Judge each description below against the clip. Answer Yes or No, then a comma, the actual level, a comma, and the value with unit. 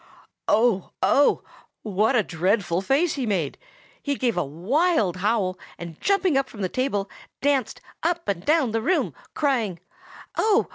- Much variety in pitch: Yes, wide, 7.3 semitones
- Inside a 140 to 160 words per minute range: Yes, average, 150 wpm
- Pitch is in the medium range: No, high, 225 Hz